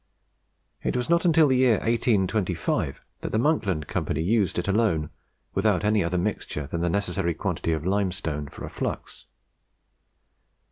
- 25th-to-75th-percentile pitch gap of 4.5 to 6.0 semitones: Yes, average, 5.1 semitones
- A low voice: Yes, low, 100 Hz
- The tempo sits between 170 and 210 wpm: No, average, 150 wpm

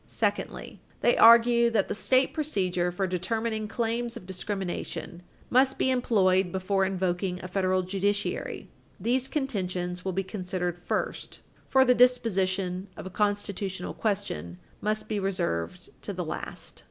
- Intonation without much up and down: No, average, 3.9 semitones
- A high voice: Yes, high, 195 Hz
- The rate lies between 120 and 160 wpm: Yes, average, 140 wpm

